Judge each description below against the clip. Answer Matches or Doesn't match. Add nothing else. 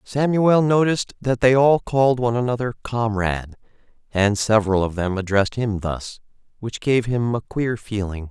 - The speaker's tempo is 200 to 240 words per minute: Doesn't match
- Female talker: Doesn't match